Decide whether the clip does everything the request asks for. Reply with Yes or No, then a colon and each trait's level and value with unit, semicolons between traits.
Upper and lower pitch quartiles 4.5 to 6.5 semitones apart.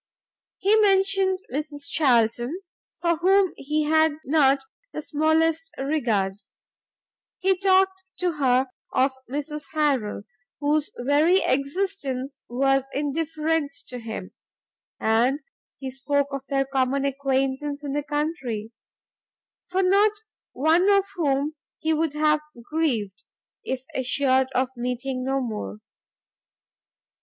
No: average, 3.6 semitones